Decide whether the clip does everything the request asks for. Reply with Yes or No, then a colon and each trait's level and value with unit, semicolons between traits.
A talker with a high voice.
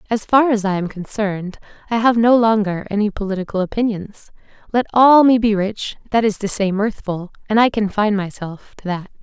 Yes: high, 210 Hz